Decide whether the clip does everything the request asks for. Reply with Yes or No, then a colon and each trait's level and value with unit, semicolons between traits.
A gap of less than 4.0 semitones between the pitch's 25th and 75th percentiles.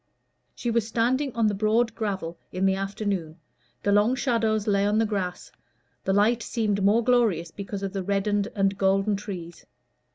Yes: narrow, 2.5 semitones